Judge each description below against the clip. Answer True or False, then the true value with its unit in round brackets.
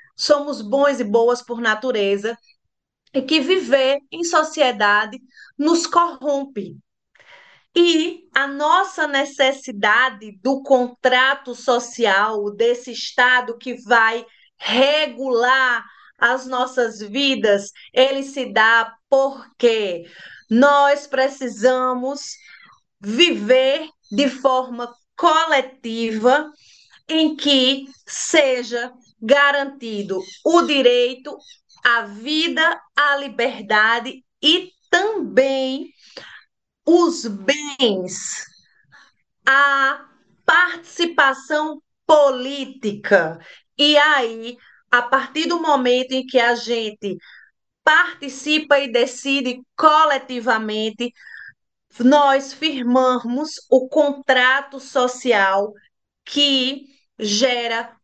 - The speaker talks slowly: True (80 wpm)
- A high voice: True (260 Hz)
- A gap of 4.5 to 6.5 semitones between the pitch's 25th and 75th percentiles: False (3.2 semitones)